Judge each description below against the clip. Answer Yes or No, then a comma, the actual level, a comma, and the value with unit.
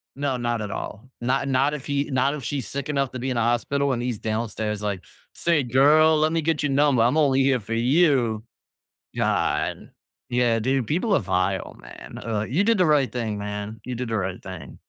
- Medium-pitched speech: No, low, 125 Hz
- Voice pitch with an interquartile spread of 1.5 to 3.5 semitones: No, average, 4.1 semitones